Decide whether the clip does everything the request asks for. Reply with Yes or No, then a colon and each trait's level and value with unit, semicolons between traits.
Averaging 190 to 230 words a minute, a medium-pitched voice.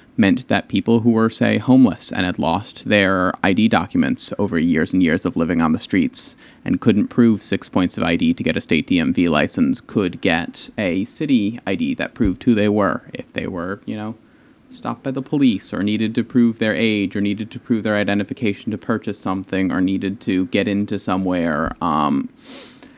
No: average, 200 wpm; low, 115 Hz